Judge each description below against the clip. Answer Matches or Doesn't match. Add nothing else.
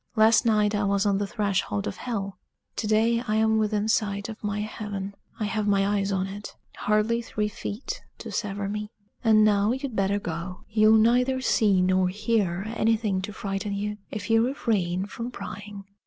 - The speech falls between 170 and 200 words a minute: Matches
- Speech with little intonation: Matches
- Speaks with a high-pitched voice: Matches